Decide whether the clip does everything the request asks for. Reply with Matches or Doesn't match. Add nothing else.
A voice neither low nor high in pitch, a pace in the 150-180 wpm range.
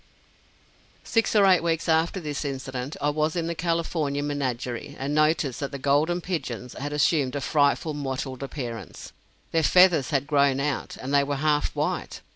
Matches